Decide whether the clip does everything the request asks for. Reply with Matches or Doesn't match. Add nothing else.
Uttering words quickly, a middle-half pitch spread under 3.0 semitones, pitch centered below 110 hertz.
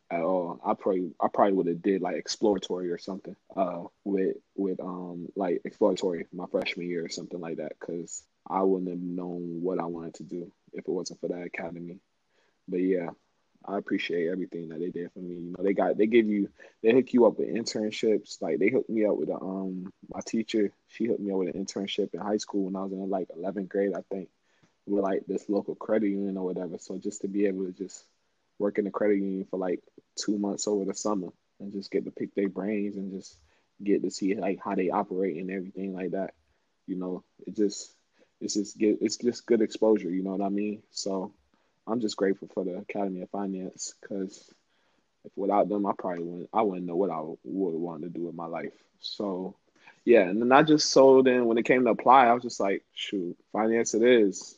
Matches